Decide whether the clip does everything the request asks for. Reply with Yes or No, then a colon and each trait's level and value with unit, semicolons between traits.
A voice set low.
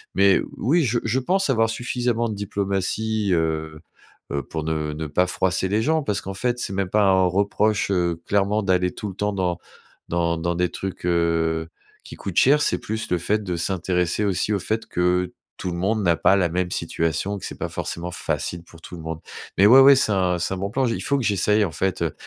Yes: very low, 95 Hz